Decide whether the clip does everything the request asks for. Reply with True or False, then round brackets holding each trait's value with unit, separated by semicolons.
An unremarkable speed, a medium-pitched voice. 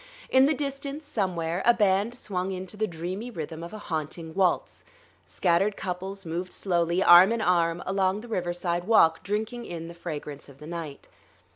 True (170 wpm; 180 Hz)